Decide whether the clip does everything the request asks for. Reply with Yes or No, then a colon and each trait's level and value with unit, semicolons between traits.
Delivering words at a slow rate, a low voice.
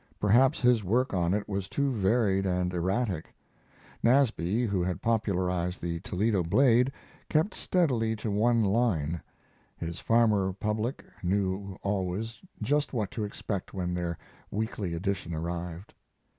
Yes: slow, 130 wpm; low, 100 Hz